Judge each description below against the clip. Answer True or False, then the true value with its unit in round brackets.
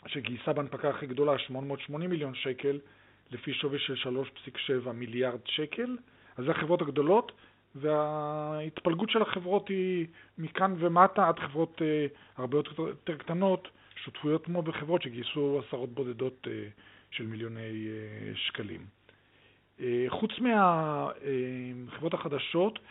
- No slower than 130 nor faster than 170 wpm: False (105 wpm)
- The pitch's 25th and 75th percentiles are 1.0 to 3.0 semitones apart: False (5.0 semitones)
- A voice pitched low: False (145 Hz)